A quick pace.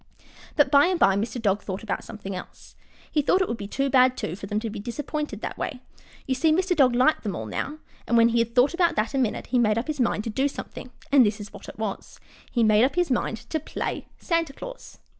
Yes: fast, 255 wpm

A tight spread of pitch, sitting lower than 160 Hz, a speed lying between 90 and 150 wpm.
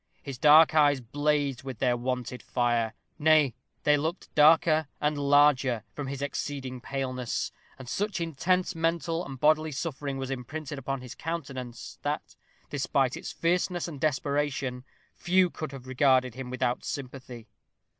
No: average, 3.4 semitones; medium, 140 Hz; average, 145 wpm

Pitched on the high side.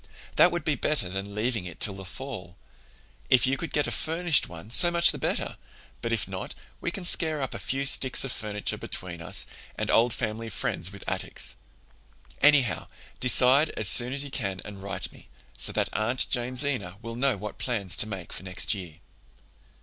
No: low, 115 Hz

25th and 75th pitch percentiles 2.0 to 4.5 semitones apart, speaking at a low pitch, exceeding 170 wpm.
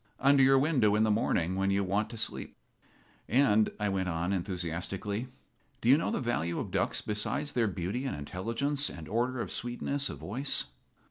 No: wide, 5.4 semitones; low, 110 Hz; average, 185 wpm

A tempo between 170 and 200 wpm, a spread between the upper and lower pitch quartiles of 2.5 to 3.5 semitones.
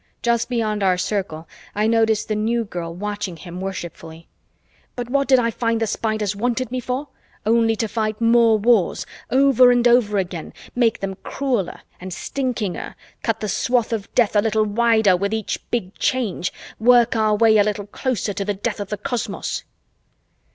Yes: average, 175 wpm; average, 2.9 semitones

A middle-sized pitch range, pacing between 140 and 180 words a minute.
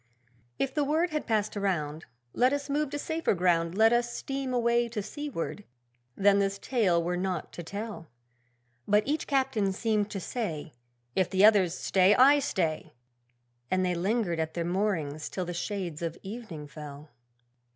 No: wide, 5.8 semitones; average, 165 wpm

